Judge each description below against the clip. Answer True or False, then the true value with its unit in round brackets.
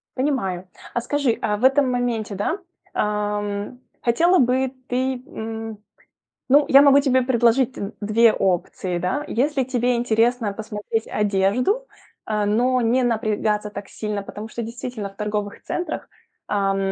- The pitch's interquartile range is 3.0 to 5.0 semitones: True (3.6 semitones)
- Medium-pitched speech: False (225 Hz)